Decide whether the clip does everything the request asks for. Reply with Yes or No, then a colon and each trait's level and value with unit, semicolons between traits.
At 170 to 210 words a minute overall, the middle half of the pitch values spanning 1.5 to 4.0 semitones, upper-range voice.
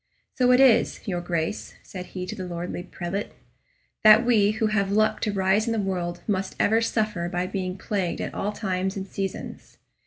Yes: average, 190 wpm; average, 2.9 semitones; high, 195 Hz